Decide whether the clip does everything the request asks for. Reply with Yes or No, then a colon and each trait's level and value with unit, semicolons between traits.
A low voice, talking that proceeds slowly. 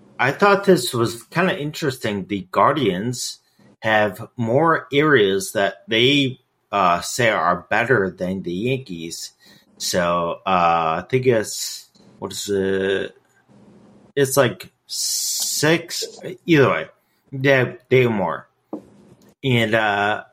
Yes: low, 125 Hz; slow, 115 wpm